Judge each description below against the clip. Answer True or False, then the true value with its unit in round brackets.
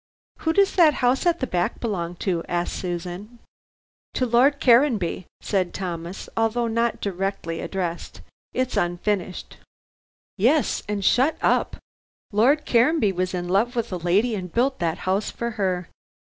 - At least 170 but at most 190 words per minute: False (145 wpm)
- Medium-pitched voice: False (205 Hz)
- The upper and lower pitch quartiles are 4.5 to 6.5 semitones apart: True (5.3 semitones)